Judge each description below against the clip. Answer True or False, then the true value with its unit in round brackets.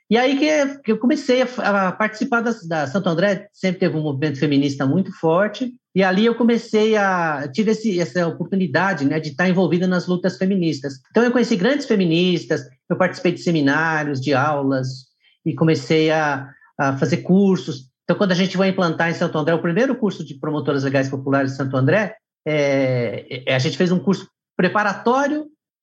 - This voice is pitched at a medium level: True (180 Hz)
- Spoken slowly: False (180 wpm)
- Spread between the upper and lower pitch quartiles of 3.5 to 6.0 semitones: True (5.3 semitones)